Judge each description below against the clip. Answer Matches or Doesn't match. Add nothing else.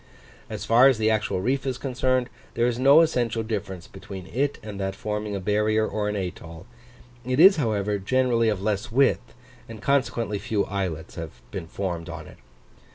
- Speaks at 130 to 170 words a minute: Doesn't match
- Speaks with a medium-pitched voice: Doesn't match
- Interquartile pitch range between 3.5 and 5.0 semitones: Matches